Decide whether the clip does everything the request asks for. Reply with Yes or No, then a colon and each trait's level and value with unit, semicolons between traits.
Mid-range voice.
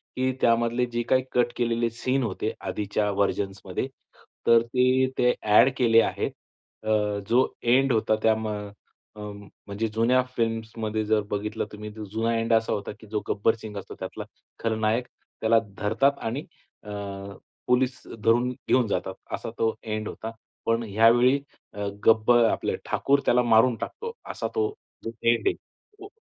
No: low, 115 Hz